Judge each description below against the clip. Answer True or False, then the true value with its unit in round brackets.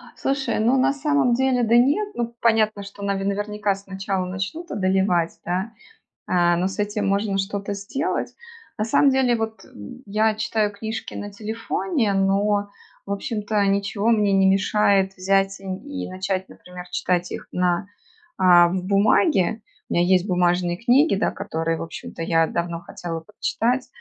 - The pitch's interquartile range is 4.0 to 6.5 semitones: False (3.0 semitones)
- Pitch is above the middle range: True (200 Hz)